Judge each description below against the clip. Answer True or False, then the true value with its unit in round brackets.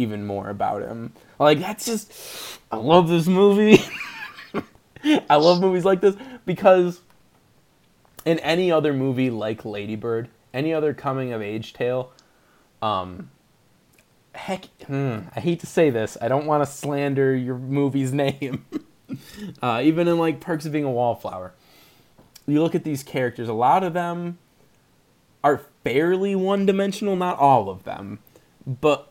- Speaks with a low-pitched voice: False (145 Hz)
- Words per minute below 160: True (145 wpm)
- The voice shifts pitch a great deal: True (5.8 semitones)